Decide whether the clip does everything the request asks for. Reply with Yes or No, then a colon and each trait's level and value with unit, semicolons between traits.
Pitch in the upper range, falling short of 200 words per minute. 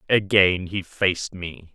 No: very low, 90 Hz; slow, 135 wpm